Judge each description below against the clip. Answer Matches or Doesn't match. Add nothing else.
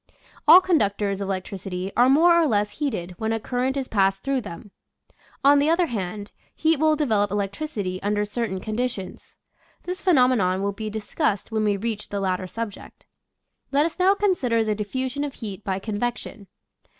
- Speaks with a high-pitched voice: Matches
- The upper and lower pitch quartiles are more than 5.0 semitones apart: Matches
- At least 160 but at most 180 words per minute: Matches